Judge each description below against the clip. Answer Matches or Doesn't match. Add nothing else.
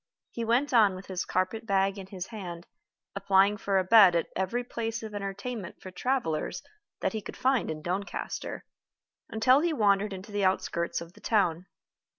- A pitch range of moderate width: Matches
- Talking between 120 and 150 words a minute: Doesn't match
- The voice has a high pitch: Matches